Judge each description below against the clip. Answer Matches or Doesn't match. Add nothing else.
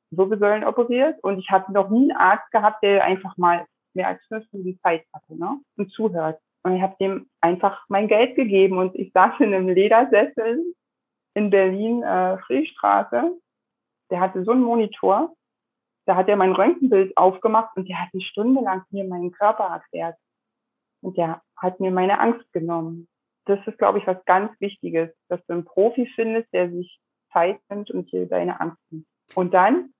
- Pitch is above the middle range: Matches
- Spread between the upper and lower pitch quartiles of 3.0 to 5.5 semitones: Matches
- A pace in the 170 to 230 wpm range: Matches